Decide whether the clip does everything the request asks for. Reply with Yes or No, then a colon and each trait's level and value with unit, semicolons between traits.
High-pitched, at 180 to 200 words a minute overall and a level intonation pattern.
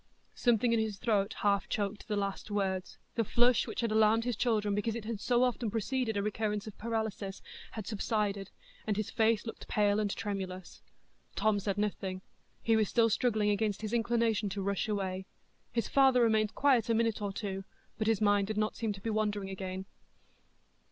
Yes: high, 215 Hz; average, 190 wpm; narrow, 2.1 semitones